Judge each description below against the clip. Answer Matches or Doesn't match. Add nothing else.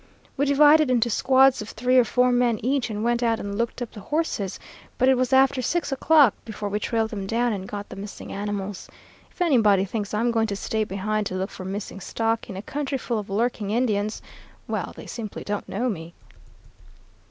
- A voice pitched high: Matches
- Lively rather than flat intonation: Doesn't match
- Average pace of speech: Doesn't match